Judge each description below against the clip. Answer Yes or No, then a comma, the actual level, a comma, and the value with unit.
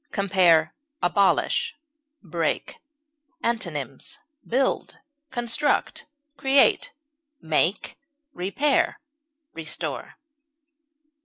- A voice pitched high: Yes, high, 195 Hz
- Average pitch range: No, wide, 8.1 semitones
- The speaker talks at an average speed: No, slow, 55 wpm